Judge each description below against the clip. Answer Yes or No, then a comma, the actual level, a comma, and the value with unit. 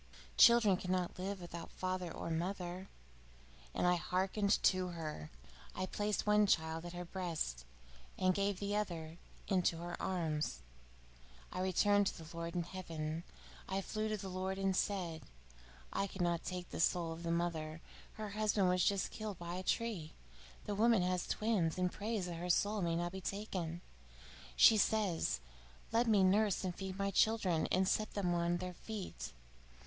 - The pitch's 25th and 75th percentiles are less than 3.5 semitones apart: Yes, average, 2.8 semitones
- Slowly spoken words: No, average, 170 wpm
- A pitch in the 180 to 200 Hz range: Yes, medium, 185 Hz